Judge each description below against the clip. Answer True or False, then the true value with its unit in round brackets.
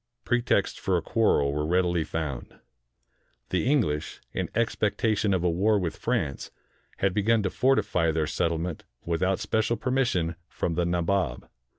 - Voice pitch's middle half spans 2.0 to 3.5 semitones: False (4.6 semitones)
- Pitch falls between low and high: False (90 Hz)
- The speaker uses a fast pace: False (145 wpm)